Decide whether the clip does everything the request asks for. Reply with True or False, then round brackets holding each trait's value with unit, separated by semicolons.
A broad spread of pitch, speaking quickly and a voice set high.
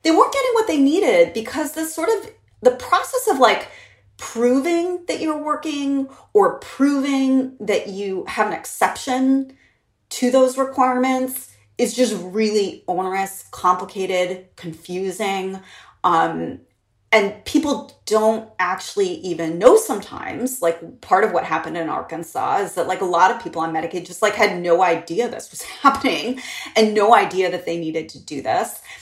False (7.4 semitones; 155 wpm; 240 Hz)